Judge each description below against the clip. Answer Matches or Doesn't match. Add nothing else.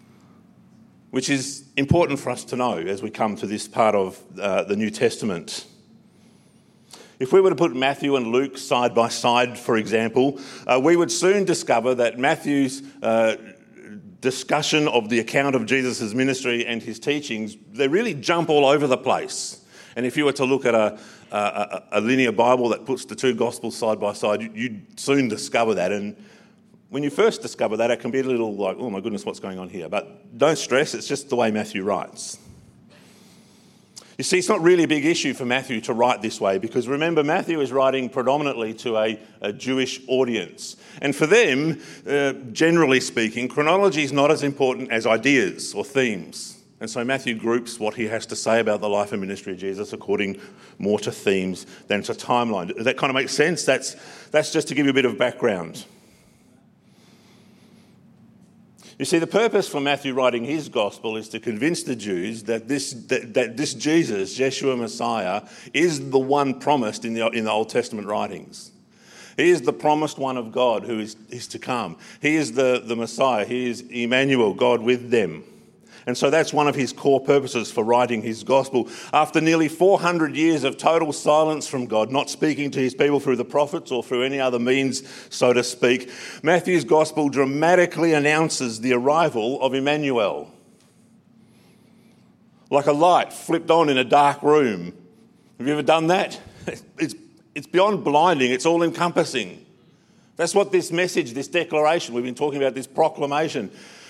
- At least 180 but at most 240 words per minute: Matches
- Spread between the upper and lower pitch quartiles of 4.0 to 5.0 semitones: Matches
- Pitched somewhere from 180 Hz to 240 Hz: Doesn't match